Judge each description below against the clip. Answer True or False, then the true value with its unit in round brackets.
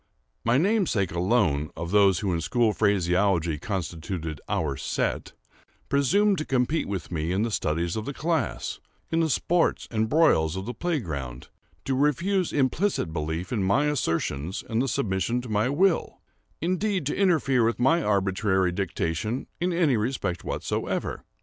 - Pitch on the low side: True (110 Hz)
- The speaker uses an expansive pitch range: True (9.0 semitones)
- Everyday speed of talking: True (145 wpm)